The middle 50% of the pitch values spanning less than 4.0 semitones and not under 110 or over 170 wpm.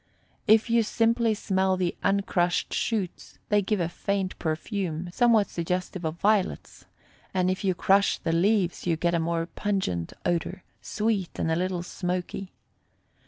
Yes: average, 3.0 semitones; average, 150 wpm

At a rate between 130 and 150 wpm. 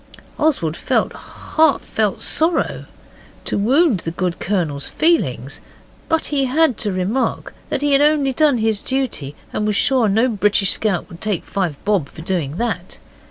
No: average, 165 wpm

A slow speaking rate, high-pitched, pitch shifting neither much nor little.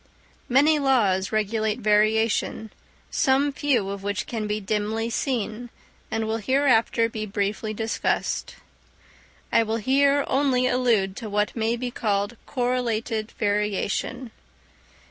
Yes: slow, 120 wpm; high, 225 Hz; average, 3.1 semitones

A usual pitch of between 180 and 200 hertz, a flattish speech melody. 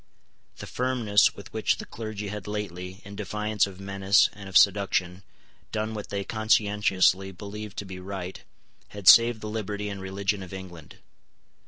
No: low, 100 Hz; narrow, 1.8 semitones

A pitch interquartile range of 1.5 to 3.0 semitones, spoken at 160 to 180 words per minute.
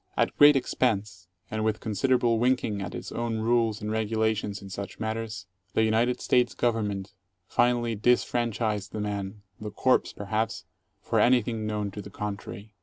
Yes: narrow, 2.4 semitones; average, 170 wpm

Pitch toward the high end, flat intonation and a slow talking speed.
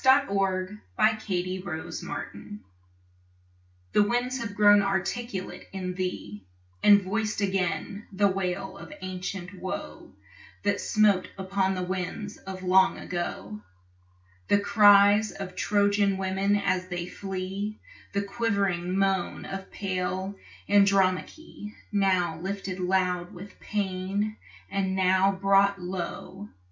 Yes: high, 195 Hz; narrow, 1.6 semitones; slow, 110 wpm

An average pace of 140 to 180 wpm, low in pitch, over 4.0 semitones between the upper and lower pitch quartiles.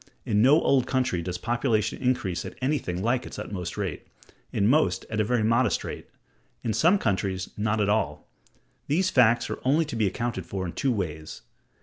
No: average, 190 wpm; low, 110 Hz; average, 5.2 semitones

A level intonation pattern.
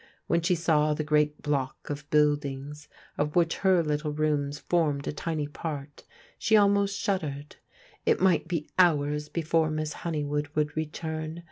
Yes: narrow, 2.1 semitones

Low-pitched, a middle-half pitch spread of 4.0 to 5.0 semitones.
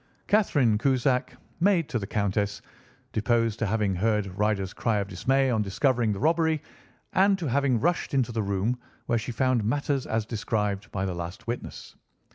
Yes: low, 115 Hz; average, 4.5 semitones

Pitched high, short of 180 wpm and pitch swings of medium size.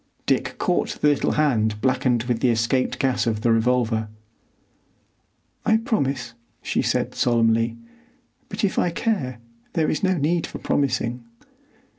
No: low, 125 Hz; average, 140 wpm; average, 4.7 semitones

